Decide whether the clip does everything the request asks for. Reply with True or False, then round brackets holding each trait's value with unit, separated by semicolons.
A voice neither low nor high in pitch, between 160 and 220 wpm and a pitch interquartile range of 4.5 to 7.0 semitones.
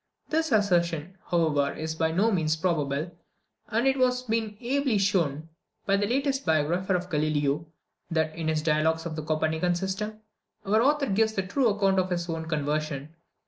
True (175 Hz; 170 wpm; 5.2 semitones)